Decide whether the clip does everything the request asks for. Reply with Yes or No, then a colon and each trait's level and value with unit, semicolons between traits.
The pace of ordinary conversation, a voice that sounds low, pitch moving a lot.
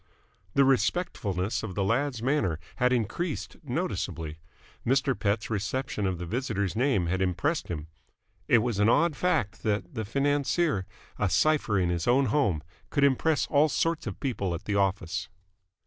Yes: average, 160 wpm; low, 115 Hz; wide, 6.7 semitones